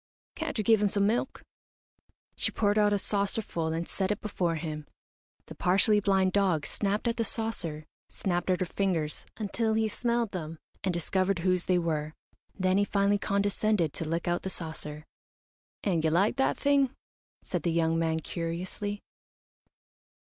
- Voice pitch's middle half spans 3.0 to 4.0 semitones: Yes, average, 3.7 semitones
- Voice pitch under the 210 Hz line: Yes, high, 190 Hz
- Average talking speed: Yes, average, 170 wpm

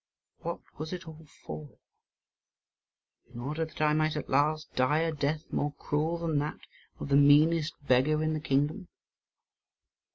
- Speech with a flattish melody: Yes, narrow, 1.7 semitones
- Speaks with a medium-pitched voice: Yes, medium, 155 Hz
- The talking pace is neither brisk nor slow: Yes, average, 155 wpm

